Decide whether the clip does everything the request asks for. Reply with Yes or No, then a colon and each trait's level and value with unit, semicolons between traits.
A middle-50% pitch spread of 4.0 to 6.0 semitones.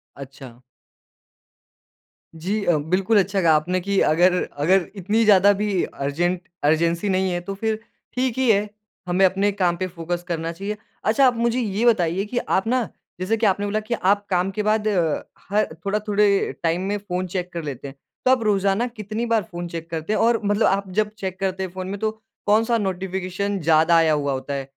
No: average, 3.4 semitones